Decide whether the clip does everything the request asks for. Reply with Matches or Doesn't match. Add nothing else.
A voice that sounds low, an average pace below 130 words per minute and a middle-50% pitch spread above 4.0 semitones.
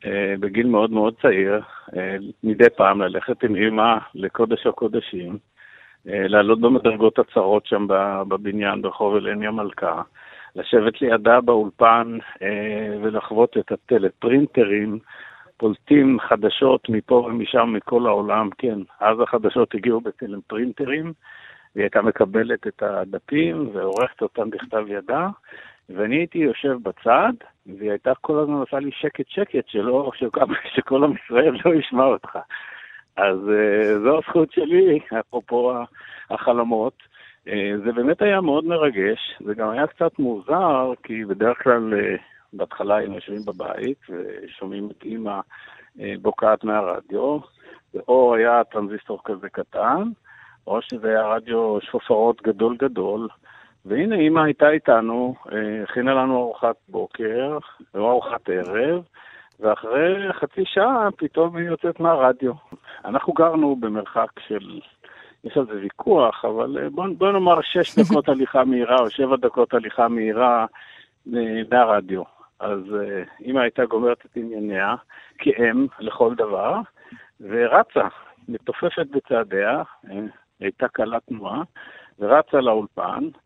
Matches